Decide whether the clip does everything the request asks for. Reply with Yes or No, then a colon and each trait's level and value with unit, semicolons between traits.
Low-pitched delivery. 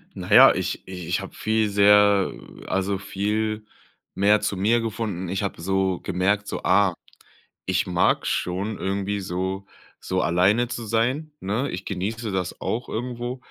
Yes: low, 100 Hz